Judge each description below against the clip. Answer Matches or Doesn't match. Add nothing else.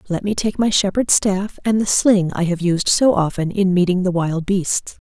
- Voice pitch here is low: Doesn't match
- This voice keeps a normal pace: Doesn't match